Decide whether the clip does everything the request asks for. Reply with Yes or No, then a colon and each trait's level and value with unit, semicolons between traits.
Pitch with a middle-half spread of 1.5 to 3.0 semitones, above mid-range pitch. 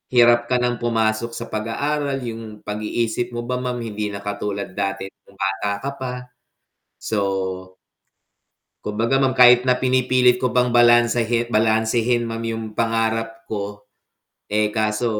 No: narrow, 2.4 semitones; low, 115 Hz